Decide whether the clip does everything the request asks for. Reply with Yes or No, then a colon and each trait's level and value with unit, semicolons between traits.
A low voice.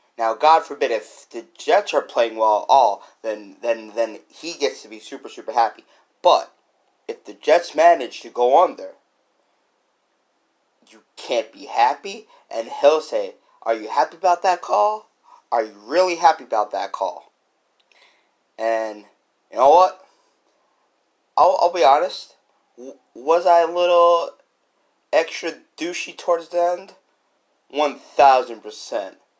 No: medium, 170 Hz